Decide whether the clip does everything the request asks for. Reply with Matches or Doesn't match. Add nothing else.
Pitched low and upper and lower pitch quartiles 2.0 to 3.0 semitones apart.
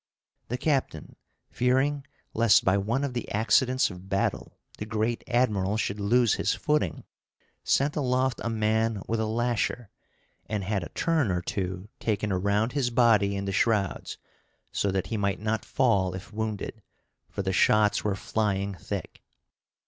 Doesn't match